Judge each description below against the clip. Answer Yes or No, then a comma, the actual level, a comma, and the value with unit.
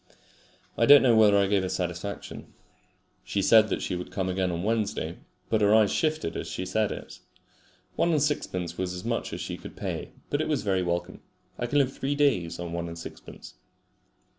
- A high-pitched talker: No, low, 100 Hz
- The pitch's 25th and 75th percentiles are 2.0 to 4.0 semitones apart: No, average, 5.2 semitones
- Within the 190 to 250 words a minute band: Yes, fast, 205 wpm